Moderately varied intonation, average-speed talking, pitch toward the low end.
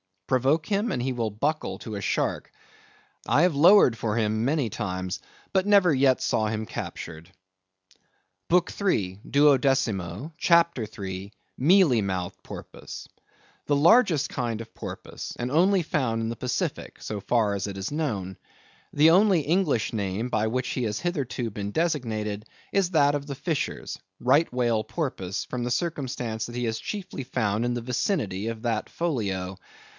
No: wide, 6.2 semitones; average, 155 wpm; low, 125 Hz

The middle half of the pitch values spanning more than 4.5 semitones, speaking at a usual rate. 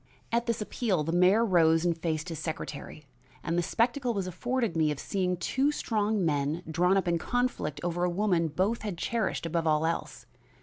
Yes: average, 4.9 semitones; average, 190 wpm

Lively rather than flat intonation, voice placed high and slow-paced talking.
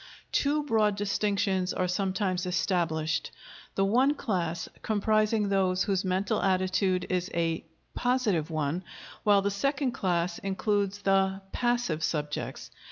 No: narrow, 2.6 semitones; high, 195 Hz; slow, 120 wpm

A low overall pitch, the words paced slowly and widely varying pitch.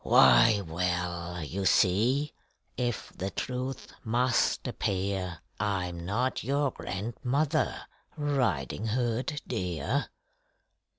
Yes: low, 105 Hz; slow, 85 wpm; wide, 6.0 semitones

